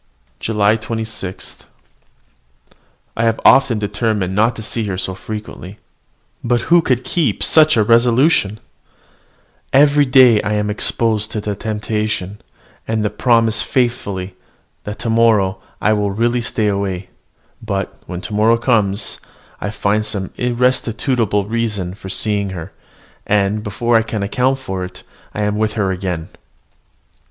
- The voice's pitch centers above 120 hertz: No, low, 110 Hz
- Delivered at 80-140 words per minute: Yes, slow, 135 wpm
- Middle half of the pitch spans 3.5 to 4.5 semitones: No, narrow, 2.5 semitones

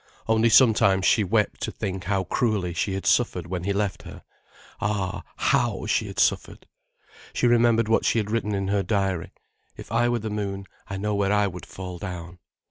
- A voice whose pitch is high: No, low, 100 Hz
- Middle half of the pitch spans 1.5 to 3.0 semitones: Yes, average, 2.7 semitones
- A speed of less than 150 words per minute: No, average, 190 wpm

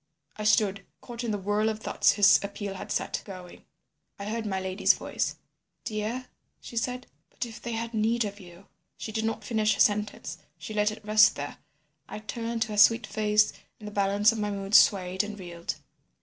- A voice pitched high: Yes, high, 210 Hz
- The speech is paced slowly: No, average, 200 wpm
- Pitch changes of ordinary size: No, narrow, 1.7 semitones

